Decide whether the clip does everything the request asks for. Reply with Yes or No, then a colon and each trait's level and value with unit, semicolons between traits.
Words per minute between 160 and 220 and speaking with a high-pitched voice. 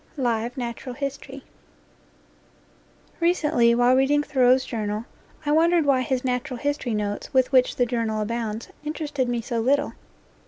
No: slow, 135 wpm; very high, 255 Hz